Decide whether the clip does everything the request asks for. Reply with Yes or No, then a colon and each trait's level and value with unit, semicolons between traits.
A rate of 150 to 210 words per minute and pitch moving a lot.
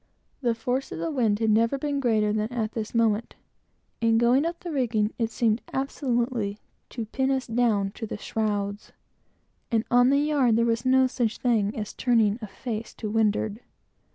No: average, 180 wpm; average, 3.0 semitones